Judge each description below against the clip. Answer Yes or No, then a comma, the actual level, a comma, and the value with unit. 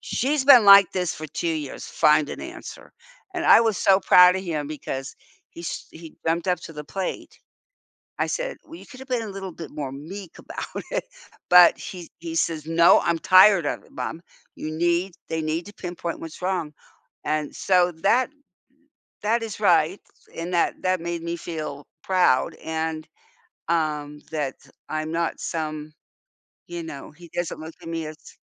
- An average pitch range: Yes, average, 3.1 semitones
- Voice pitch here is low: No, medium, 170 Hz